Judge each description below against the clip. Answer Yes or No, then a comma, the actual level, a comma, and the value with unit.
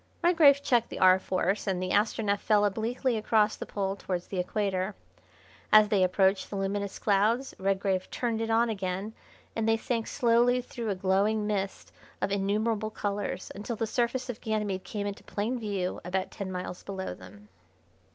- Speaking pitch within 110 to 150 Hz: No, high, 205 Hz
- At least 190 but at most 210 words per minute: No, average, 170 wpm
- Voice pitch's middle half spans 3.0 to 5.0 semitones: No, narrow, 2.6 semitones